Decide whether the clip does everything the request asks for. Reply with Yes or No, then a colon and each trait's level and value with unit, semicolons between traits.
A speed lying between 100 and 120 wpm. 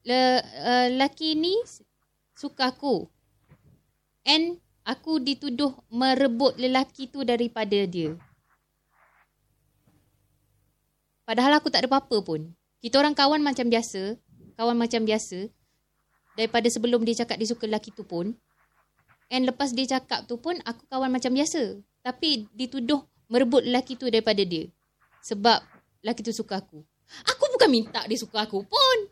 No: average, 135 wpm